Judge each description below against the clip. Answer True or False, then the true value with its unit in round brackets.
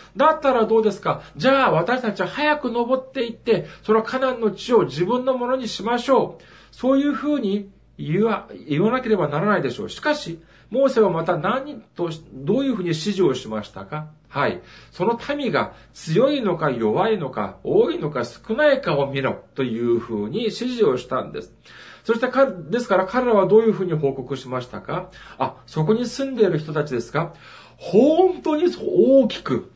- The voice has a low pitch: False (215 Hz)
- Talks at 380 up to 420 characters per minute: False (355 characters per minute)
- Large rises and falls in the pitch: True (8.0 semitones)